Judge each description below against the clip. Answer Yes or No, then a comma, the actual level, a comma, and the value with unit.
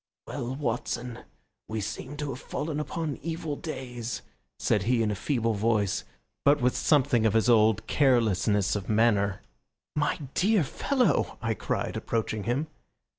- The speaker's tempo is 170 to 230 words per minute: No, average, 145 wpm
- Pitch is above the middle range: No, low, 120 Hz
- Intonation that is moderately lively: Yes, average, 4.9 semitones